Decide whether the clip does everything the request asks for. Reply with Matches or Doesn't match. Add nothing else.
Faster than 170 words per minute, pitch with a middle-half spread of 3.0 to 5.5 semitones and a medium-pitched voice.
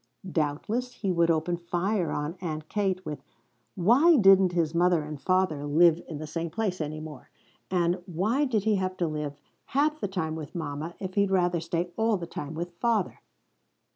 Matches